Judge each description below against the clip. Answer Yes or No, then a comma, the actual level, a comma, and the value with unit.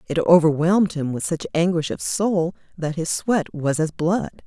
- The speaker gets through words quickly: No, average, 190 wpm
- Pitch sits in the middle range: Yes, medium, 170 Hz